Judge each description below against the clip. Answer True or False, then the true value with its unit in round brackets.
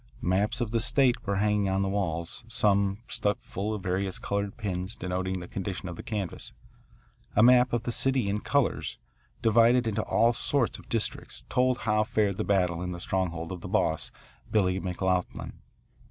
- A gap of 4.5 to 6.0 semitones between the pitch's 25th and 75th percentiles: False (3.6 semitones)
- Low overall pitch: True (100 Hz)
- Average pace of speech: True (180 wpm)